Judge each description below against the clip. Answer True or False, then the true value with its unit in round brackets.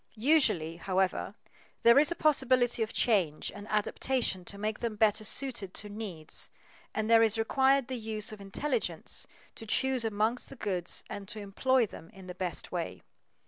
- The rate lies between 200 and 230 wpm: False (170 wpm)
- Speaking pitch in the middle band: False (215 Hz)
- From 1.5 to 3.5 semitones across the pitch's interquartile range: False (4.2 semitones)